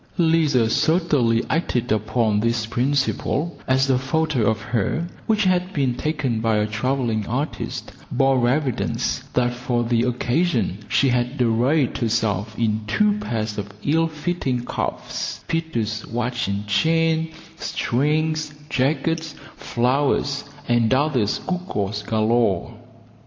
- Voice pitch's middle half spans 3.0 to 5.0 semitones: No, wide, 5.4 semitones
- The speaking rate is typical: No, slow, 120 wpm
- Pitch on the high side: No, low, 125 Hz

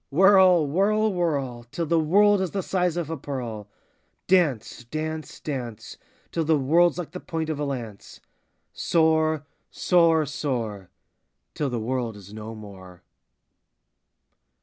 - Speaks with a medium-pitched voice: Yes, medium, 155 Hz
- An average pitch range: No, wide, 6.3 semitones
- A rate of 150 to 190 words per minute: No, average, 140 wpm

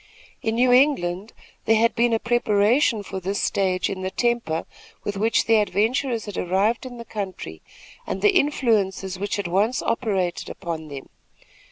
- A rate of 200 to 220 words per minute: No, average, 165 wpm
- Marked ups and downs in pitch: No, average, 3.7 semitones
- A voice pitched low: No, high, 205 Hz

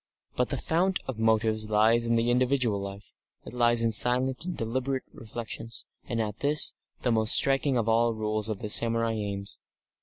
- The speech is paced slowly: No, average, 185 wpm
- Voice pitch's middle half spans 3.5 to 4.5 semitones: No, narrow, 2.5 semitones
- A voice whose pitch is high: No, low, 115 Hz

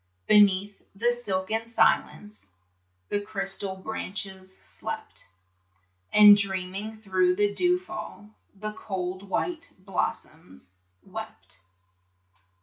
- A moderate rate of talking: No, slow, 90 wpm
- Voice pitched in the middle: No, high, 200 Hz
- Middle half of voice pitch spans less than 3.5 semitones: Yes, narrow, 2.4 semitones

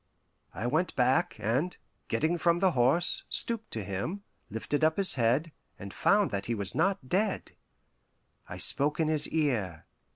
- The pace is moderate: Yes, average, 160 wpm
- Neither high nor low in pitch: Yes, medium, 150 Hz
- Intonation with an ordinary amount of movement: No, wide, 7.2 semitones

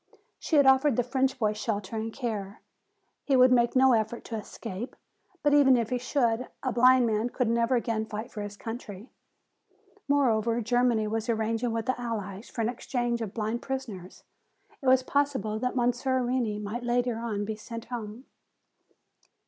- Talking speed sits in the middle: Yes, average, 175 wpm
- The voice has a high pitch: Yes, high, 235 Hz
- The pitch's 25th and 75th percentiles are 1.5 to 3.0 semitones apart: Yes, narrow, 2.5 semitones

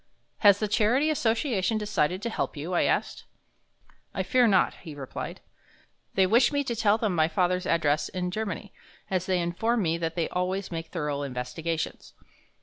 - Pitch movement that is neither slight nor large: Yes, average, 4.9 semitones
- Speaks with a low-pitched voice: No, medium, 185 Hz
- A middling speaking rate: Yes, average, 170 wpm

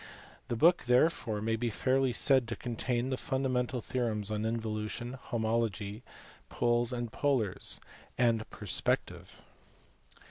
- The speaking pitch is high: No, low, 120 Hz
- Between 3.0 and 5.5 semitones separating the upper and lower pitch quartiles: No, narrow, 2.5 semitones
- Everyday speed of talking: No, slow, 120 wpm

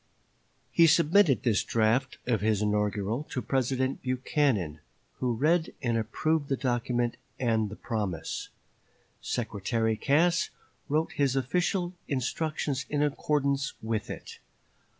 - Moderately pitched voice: No, low, 130 Hz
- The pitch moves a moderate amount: Yes, average, 4.8 semitones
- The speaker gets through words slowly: Yes, slow, 115 wpm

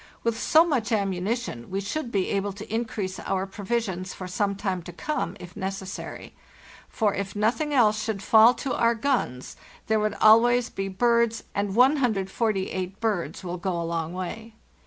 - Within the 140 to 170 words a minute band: Yes, average, 165 wpm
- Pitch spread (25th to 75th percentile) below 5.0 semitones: Yes, average, 3.6 semitones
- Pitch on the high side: Yes, high, 205 Hz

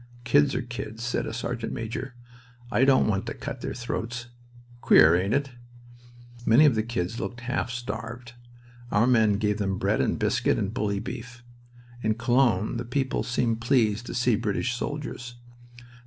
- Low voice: Yes, low, 120 Hz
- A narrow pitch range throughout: Yes, narrow, 2.3 semitones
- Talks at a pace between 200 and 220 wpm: No, average, 165 wpm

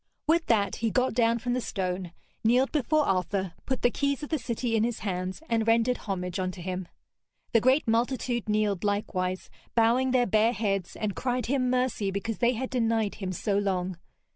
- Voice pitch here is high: Yes, high, 225 Hz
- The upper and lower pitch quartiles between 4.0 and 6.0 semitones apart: Yes, average, 4.3 semitones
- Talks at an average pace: Yes, average, 190 wpm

